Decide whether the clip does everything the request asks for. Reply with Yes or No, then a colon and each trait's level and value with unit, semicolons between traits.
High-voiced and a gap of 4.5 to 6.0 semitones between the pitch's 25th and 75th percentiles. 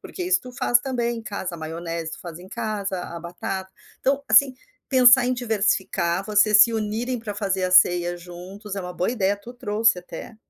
Yes: high, 205 Hz; average, 4.9 semitones